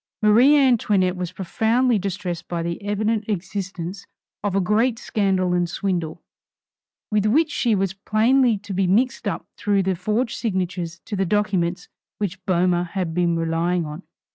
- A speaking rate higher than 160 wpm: No, average, 155 wpm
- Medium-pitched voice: No, high, 195 Hz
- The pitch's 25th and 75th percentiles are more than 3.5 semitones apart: No, average, 3.1 semitones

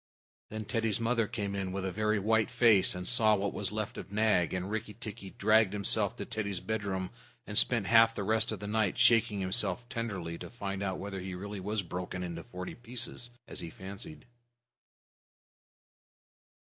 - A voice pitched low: Yes, low, 105 Hz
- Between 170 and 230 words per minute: Yes, average, 180 wpm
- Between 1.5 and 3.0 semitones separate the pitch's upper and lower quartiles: Yes, average, 2.7 semitones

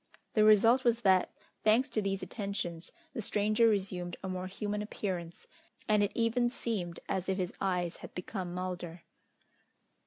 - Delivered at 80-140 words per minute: No, average, 155 wpm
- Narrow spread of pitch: No, average, 3.0 semitones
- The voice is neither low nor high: No, high, 195 Hz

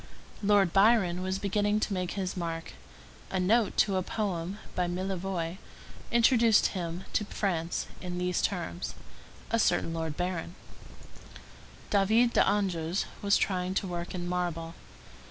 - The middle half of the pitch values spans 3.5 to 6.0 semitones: No, narrow, 2.5 semitones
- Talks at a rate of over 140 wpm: No, slow, 135 wpm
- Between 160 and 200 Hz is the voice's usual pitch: Yes, medium, 185 Hz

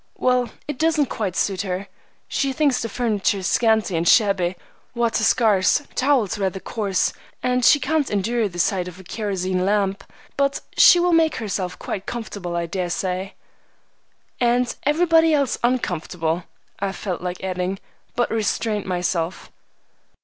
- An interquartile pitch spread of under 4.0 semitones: No, average, 5.3 semitones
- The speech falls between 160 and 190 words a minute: No, average, 145 wpm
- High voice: Yes, high, 205 Hz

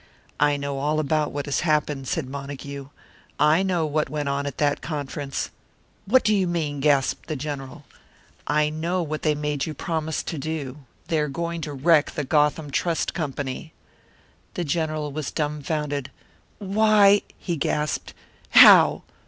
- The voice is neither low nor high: Yes, medium, 150 Hz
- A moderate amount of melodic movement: No, narrow, 2.2 semitones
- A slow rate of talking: No, average, 155 wpm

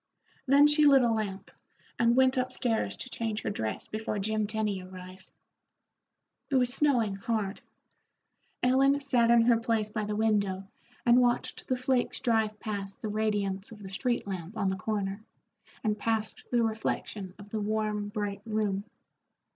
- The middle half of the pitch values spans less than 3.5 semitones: Yes, average, 2.9 semitones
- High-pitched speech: Yes, high, 215 Hz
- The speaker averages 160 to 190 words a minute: Yes, average, 165 wpm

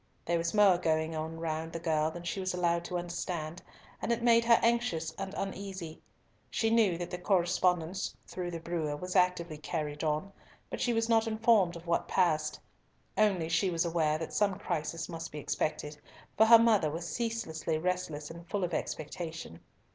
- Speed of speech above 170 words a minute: Yes, average, 185 wpm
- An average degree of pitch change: Yes, average, 3.4 semitones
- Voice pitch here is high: No, medium, 175 Hz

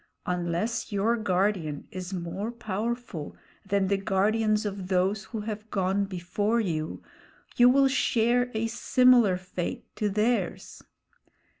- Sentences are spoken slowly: Yes, slow, 125 wpm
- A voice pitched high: Yes, high, 205 Hz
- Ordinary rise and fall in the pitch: Yes, average, 3.6 semitones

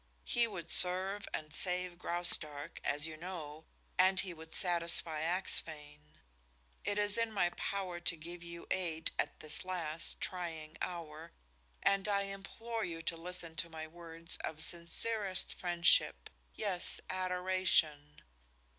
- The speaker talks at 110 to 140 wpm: Yes, slow, 135 wpm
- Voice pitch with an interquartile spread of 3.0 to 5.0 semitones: No, narrow, 2.6 semitones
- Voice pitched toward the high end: No, medium, 175 Hz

